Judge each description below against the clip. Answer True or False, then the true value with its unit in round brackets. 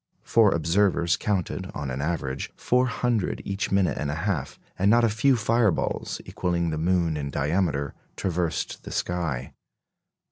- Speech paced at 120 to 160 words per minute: True (150 wpm)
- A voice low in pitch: True (90 Hz)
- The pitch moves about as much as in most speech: True (4.9 semitones)